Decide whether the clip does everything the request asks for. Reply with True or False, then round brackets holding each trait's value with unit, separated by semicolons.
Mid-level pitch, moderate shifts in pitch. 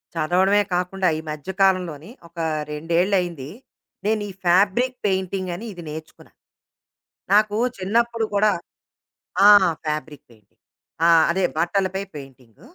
True (180 Hz; 4.0 semitones)